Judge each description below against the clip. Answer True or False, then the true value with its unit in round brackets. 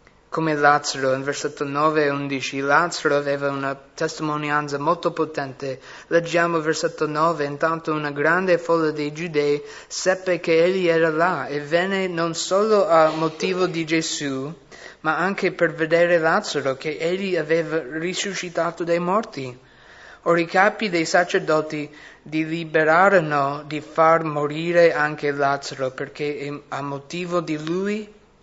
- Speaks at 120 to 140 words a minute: True (135 wpm)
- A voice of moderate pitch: True (160 Hz)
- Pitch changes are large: False (2.8 semitones)